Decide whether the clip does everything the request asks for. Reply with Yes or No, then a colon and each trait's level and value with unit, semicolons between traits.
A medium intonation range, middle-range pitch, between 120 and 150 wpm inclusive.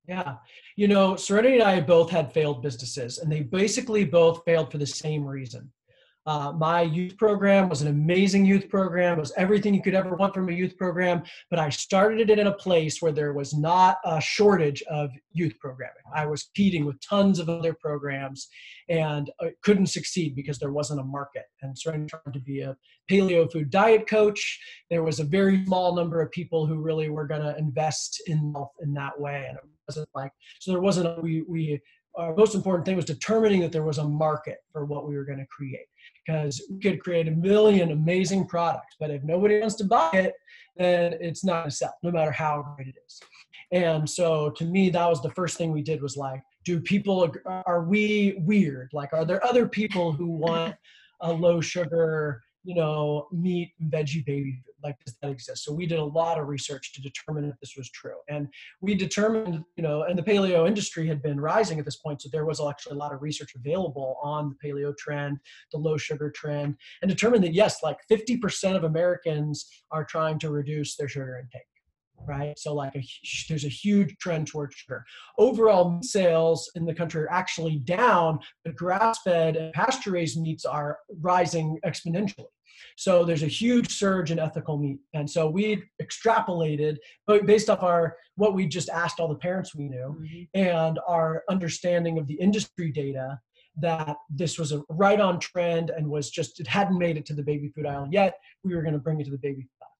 No: average, 3.7 semitones; medium, 165 Hz; fast, 205 wpm